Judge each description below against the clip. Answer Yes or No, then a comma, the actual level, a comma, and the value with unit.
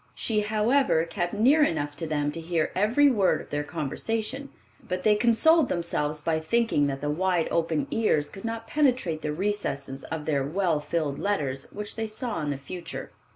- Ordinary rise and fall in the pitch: No, wide, 6.9 semitones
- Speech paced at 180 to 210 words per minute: Yes, average, 185 wpm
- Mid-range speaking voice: Yes, medium, 175 Hz